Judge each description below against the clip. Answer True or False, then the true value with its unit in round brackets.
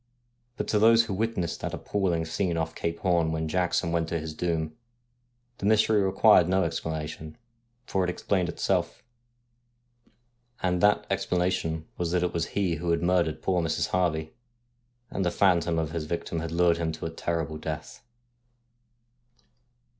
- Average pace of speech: True (160 wpm)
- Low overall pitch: True (85 Hz)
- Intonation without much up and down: True (2.3 semitones)